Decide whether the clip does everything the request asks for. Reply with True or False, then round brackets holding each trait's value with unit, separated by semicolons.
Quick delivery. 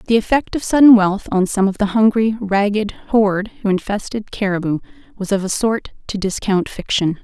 False (180 wpm)